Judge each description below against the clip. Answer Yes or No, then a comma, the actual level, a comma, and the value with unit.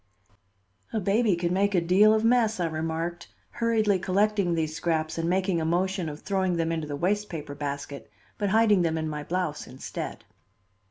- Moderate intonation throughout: Yes, average, 4.0 semitones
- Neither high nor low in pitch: Yes, medium, 175 Hz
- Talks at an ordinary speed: Yes, average, 180 wpm